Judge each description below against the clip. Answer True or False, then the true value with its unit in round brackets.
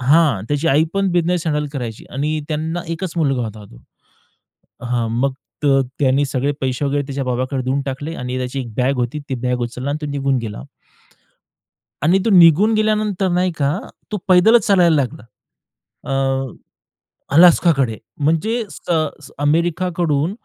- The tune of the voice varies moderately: True (4.5 semitones)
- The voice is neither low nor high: True (145 Hz)